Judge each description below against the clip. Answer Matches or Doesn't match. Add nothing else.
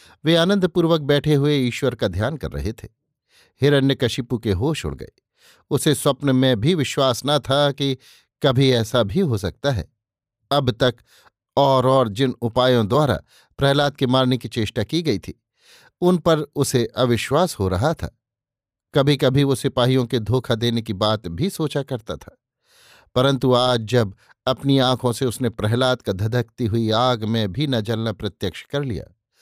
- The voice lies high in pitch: Doesn't match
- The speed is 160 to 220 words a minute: Matches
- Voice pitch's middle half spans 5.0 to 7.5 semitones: Doesn't match